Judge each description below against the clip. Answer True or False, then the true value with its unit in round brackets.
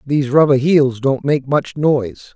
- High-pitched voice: False (140 Hz)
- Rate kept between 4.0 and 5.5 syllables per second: True (4.6 syllables/s)